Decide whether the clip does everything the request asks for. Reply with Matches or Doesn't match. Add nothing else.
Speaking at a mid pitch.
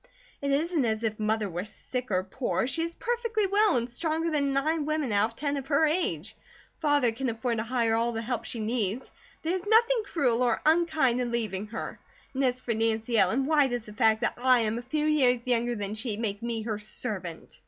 Doesn't match